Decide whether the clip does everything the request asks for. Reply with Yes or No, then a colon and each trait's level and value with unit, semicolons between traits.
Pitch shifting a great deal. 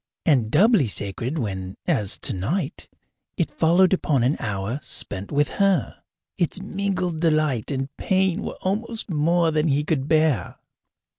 Yes: wide, 6.8 semitones